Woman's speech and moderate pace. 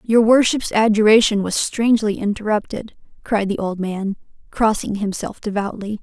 No: female; slow, 130 wpm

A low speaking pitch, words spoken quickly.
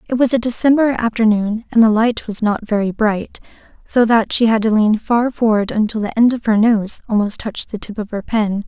No: high, 220 Hz; fast, 230 wpm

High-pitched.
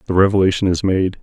No: very low, 95 Hz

